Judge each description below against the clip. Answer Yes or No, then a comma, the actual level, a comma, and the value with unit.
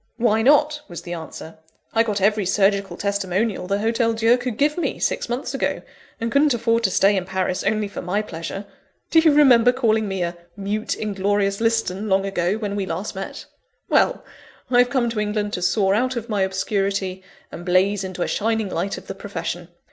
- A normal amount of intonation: Yes, average, 3.1 semitones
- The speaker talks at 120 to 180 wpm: No, average, 200 wpm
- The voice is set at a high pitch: Yes, high, 205 Hz